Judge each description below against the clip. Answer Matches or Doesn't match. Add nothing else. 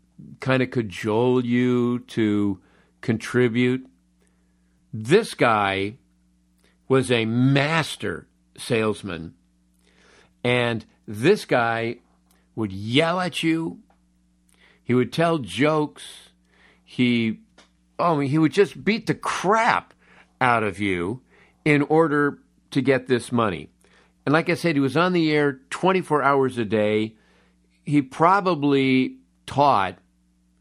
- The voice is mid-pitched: Doesn't match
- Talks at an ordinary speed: Doesn't match